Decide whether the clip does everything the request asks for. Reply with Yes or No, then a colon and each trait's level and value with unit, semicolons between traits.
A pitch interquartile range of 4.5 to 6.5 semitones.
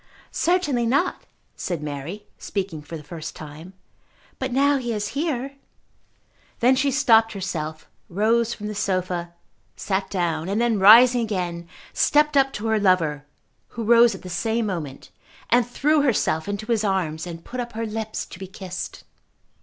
Yes: wide, 5.4 semitones